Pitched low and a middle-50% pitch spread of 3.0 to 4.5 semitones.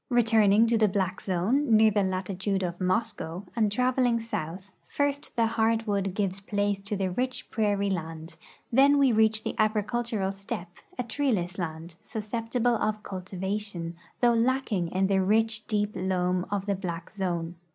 No: high, 205 Hz; average, 3.4 semitones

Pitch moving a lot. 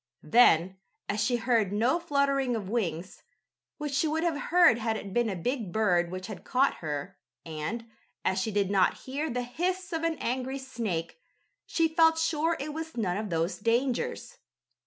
Yes: wide, 7.2 semitones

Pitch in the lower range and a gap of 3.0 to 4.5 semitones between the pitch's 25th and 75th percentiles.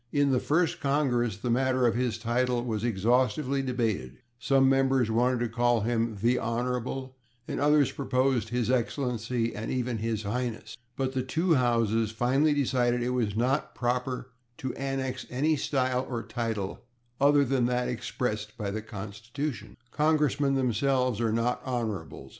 No: low, 125 Hz; narrow, 2.5 semitones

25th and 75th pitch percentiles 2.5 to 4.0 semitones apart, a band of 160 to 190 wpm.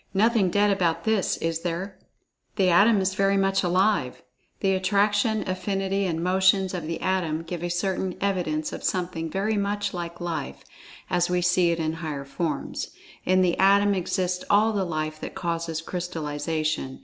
Yes: average, 2.9 semitones; average, 165 wpm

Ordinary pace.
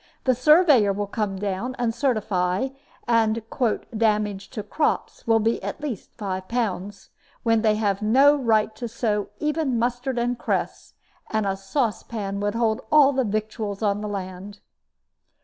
Yes: average, 155 wpm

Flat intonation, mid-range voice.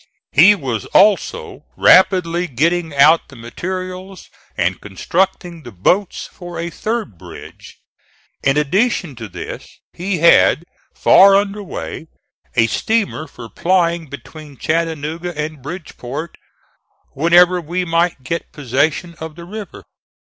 No: average, 4.1 semitones; medium, 170 Hz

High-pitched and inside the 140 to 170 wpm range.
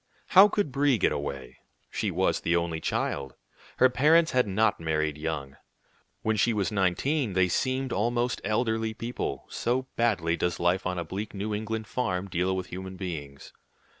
No: low, 100 Hz; average, 165 wpm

